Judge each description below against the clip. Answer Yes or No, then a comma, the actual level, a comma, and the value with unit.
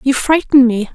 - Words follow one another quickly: No, average, 190 wpm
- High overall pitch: Yes, very high, 260 Hz